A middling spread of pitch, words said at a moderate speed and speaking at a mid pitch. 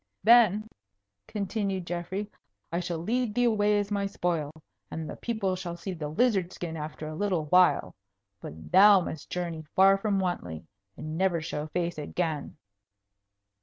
Yes: average, 4.0 semitones; average, 155 wpm; medium, 180 Hz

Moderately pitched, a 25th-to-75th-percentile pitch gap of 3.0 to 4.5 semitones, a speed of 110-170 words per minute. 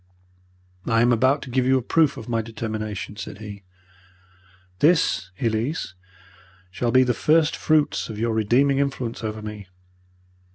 No: low, 120 Hz; average, 4.0 semitones; average, 150 wpm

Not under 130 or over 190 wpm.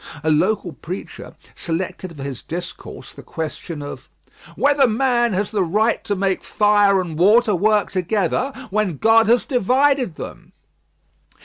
Yes: average, 140 wpm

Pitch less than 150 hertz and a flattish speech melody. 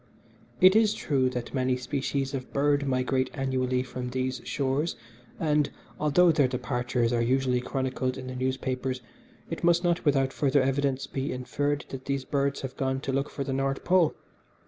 Yes: low, 135 Hz; narrow, 1.8 semitones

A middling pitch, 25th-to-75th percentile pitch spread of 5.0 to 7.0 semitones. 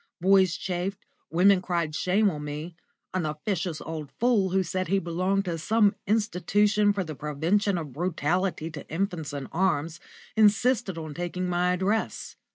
No: medium, 180 Hz; average, 3.4 semitones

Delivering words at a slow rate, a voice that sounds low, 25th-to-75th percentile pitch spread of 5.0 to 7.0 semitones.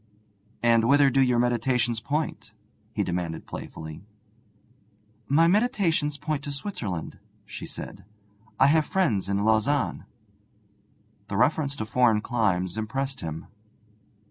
Yes: slow, 115 wpm; low, 120 Hz; wide, 5.4 semitones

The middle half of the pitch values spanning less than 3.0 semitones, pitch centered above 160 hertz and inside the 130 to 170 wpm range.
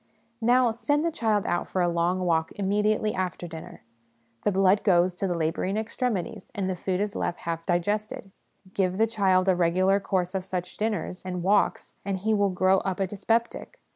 No: narrow, 2.6 semitones; high, 190 Hz; average, 190 wpm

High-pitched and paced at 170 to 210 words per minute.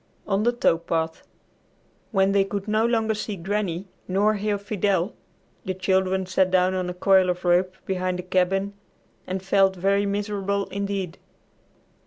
No: high, 195 Hz; average, 160 wpm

